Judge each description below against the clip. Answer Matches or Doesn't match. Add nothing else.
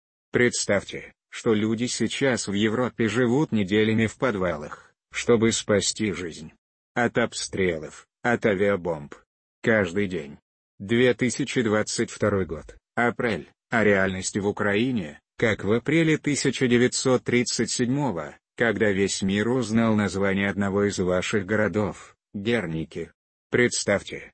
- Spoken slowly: Matches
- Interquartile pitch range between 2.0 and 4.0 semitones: Matches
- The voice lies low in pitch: Matches